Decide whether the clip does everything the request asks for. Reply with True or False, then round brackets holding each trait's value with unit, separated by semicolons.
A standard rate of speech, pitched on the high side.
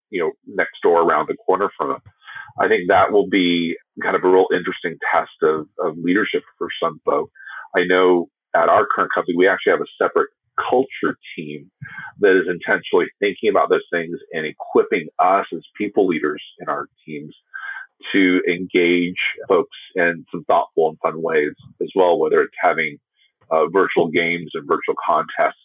True (175 wpm; 400 Hz)